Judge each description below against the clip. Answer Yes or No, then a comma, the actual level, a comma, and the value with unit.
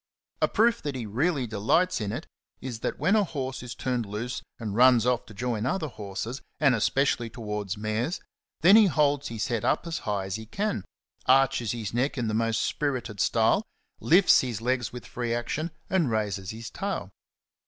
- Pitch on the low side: Yes, low, 120 Hz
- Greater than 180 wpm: Yes, average, 190 wpm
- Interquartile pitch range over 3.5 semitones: Yes, average, 4.4 semitones